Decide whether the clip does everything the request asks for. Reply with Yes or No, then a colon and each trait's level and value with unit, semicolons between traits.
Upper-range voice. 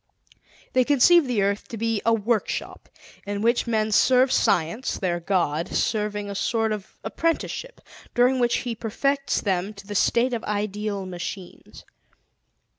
Yes: high, 215 Hz